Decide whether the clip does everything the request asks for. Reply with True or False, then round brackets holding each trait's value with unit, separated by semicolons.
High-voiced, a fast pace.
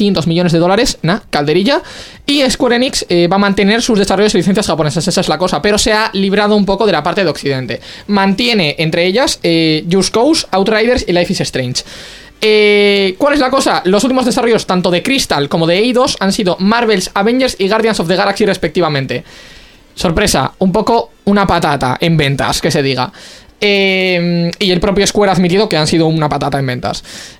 True (195 Hz; 200 wpm)